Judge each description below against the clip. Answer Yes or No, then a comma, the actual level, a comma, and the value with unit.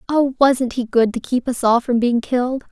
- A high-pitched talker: Yes, very high, 250 Hz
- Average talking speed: No, fast, 245 wpm